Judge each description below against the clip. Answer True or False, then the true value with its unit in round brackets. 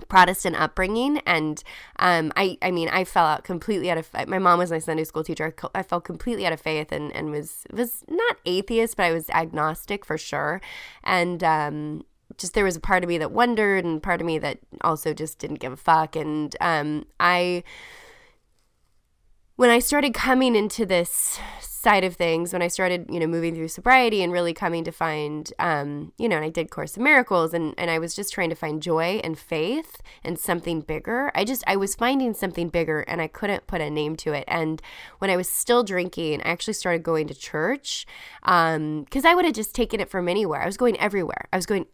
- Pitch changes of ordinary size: True (4.4 semitones)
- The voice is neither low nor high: True (175 Hz)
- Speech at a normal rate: False (220 wpm)